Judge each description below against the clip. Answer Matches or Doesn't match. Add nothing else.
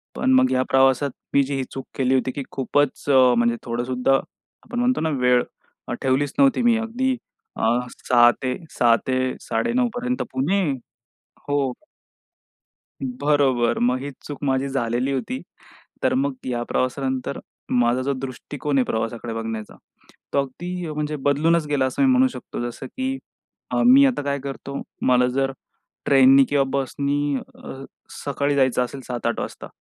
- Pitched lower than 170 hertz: Matches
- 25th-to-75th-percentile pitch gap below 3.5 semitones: Matches